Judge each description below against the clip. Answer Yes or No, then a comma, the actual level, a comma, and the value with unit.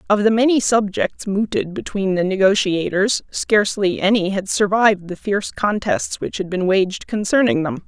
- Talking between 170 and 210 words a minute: No, average, 160 wpm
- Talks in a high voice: Yes, high, 200 Hz